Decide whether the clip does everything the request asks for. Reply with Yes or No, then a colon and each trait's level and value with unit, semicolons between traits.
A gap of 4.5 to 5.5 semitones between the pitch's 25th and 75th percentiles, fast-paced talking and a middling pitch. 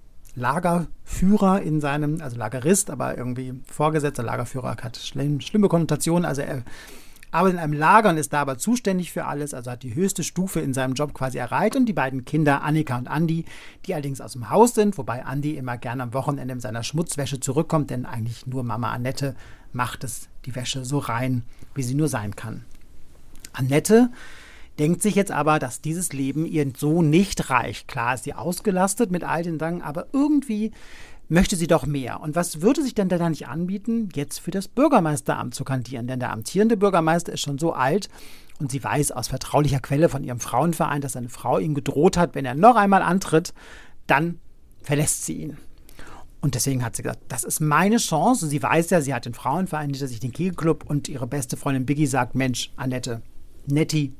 Yes: average, 4.8 semitones; fast, 195 wpm; medium, 145 Hz